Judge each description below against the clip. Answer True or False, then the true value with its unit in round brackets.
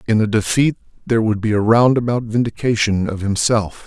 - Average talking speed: True (170 wpm)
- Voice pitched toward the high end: False (110 Hz)